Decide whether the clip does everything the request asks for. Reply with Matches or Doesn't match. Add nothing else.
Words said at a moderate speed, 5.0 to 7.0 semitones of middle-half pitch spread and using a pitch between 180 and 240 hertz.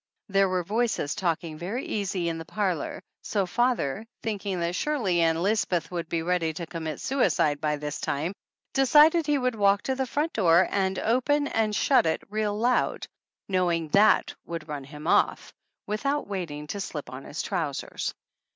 Matches